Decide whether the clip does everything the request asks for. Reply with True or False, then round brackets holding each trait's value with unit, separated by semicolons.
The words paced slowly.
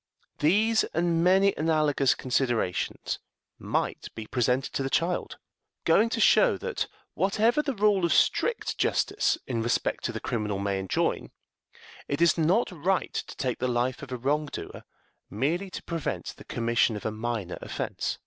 False (160 wpm)